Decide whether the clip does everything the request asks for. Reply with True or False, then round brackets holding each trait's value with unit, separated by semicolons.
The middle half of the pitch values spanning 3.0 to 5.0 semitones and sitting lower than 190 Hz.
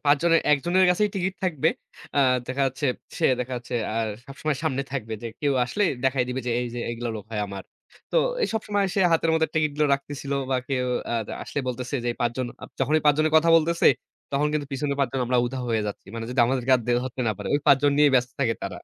True (3.9 semitones; 135 Hz)